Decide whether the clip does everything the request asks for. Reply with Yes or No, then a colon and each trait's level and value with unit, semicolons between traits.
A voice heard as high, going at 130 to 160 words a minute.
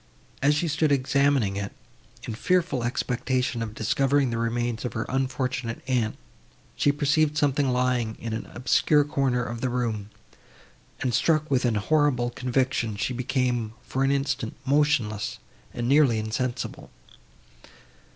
No: low, 125 Hz; average, 140 wpm